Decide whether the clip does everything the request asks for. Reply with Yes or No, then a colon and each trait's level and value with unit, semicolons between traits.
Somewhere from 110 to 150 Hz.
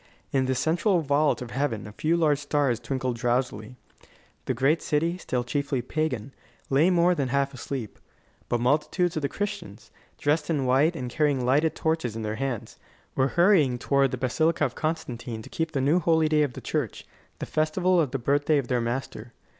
Yes: medium, 140 Hz